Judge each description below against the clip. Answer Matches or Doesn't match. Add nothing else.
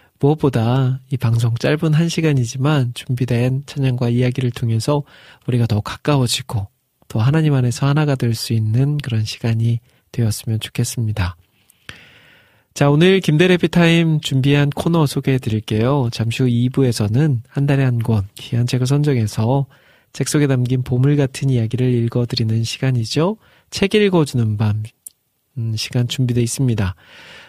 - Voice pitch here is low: Matches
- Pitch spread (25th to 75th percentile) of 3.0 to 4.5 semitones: Matches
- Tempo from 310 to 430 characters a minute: Matches